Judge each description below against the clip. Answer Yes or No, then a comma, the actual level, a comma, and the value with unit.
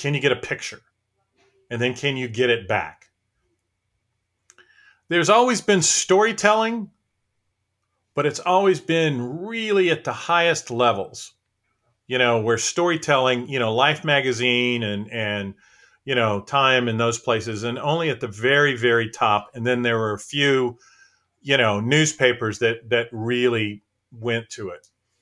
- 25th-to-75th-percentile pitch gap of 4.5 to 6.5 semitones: Yes, average, 4.9 semitones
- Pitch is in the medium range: No, low, 120 Hz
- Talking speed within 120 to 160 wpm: Yes, average, 150 wpm